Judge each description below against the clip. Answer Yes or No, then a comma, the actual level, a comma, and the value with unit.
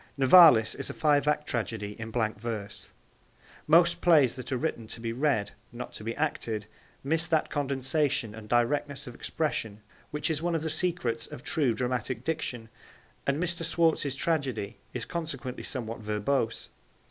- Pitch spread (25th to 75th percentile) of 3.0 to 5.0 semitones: No, wide, 5.4 semitones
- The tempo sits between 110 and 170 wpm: Yes, average, 160 wpm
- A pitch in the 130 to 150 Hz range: Yes, low, 135 Hz